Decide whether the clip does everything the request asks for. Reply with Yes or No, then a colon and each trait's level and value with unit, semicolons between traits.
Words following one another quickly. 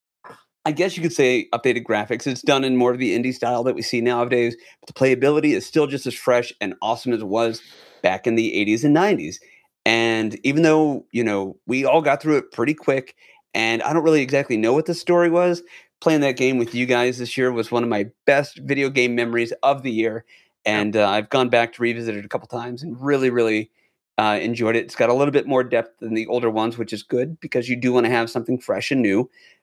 Yes: fast, 245 wpm